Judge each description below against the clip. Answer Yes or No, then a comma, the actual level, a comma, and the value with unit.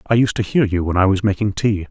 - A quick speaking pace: Yes, fast, 315 wpm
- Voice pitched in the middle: No, low, 100 Hz